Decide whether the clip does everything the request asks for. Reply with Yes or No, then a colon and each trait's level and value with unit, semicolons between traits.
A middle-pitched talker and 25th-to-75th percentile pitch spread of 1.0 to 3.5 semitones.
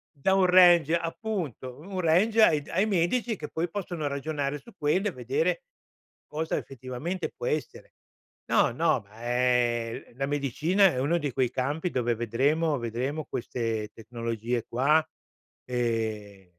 No: medium, 145 Hz; wide, 6.1 semitones